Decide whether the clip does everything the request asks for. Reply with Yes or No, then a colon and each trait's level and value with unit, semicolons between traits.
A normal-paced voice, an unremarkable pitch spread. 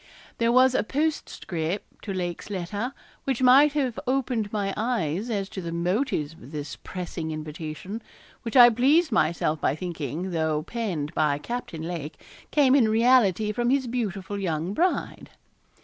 No: average, 150 wpm; wide, 7.0 semitones